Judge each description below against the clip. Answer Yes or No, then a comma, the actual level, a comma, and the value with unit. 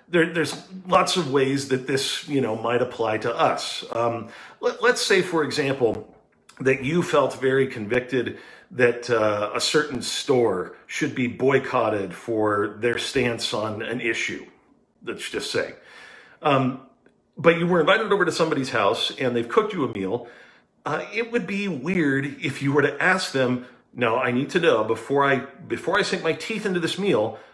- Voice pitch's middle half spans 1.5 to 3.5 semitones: No, wide, 5.5 semitones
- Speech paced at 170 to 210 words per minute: Yes, average, 180 wpm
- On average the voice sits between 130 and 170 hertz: Yes, low, 135 Hz